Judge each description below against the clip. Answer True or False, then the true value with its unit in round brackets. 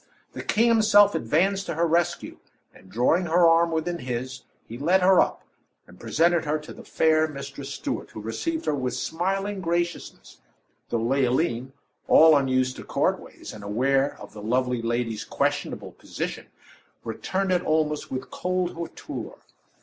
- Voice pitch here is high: False (155 Hz)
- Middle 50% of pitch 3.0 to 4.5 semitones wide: False (5.6 semitones)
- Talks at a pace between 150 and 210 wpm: True (155 wpm)